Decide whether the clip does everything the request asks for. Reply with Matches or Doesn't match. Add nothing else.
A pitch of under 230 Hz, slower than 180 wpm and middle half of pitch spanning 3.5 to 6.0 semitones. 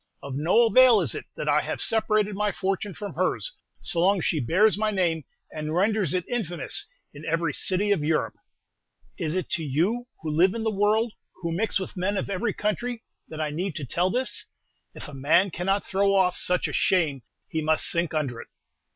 Doesn't match